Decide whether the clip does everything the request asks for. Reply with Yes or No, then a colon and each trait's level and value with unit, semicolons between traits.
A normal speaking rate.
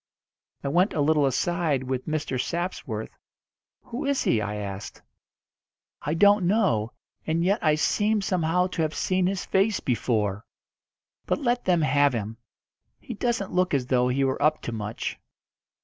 Yes: average, 160 wpm